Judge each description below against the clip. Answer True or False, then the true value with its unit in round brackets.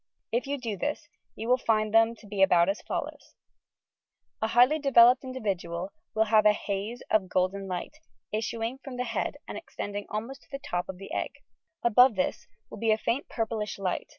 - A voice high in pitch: True (220 Hz)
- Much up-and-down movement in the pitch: False (3.8 semitones)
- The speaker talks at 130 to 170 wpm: False (190 wpm)